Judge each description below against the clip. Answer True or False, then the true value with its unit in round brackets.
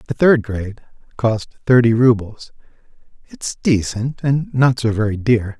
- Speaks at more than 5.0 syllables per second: False (4.4 syllables/s)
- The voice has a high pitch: False (120 Hz)